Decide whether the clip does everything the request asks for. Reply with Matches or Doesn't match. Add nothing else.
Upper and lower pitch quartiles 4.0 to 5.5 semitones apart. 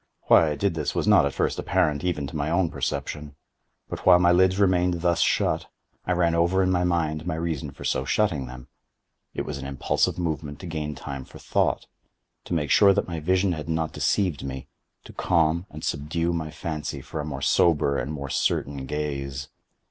Doesn't match